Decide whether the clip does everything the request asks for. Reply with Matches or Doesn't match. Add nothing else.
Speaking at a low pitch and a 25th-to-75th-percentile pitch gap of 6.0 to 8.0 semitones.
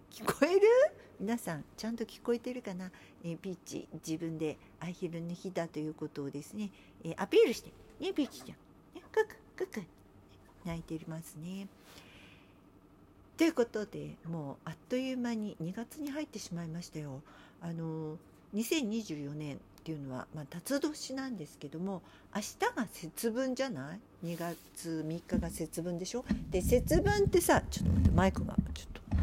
Doesn't match